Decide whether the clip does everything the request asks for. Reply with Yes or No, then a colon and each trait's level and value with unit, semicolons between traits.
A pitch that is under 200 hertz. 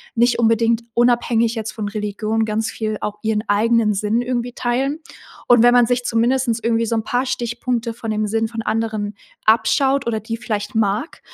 No: high, 225 Hz